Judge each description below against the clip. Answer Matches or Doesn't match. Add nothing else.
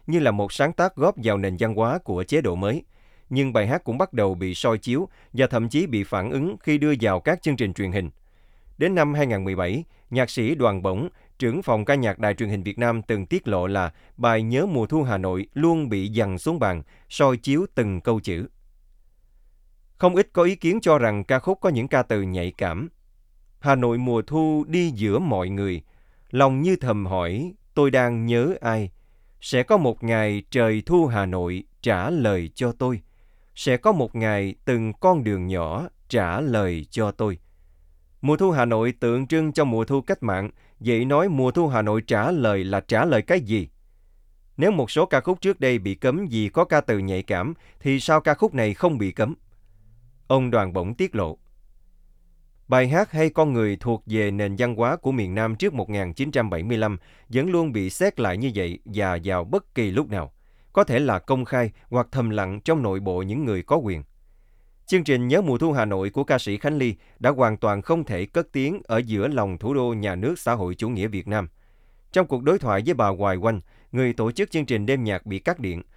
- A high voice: Doesn't match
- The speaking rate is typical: Matches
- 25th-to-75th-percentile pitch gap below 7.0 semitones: Matches